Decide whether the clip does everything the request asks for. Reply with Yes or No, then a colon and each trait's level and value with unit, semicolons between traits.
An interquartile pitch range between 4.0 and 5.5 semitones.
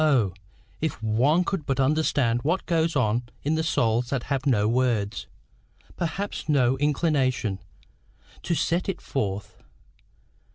Yes: average, 5.0 semitones